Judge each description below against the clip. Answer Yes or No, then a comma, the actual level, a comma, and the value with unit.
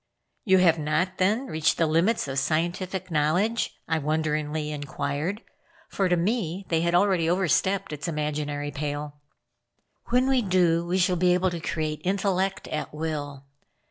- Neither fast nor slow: Yes, average, 150 wpm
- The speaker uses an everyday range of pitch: Yes, average, 3.7 semitones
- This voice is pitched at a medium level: Yes, medium, 165 Hz